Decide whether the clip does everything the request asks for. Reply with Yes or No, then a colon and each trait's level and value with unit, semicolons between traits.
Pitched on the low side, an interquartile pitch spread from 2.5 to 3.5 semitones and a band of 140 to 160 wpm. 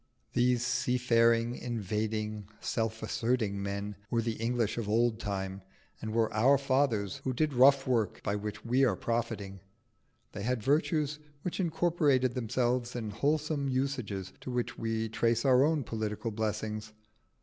Yes: low, 115 Hz; average, 3.2 semitones; average, 145 wpm